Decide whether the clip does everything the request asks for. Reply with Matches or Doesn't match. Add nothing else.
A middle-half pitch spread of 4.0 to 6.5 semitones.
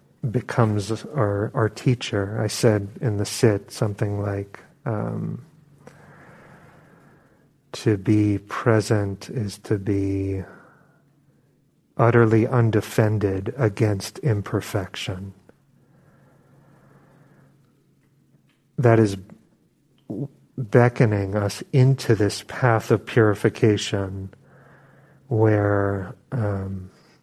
Doesn't match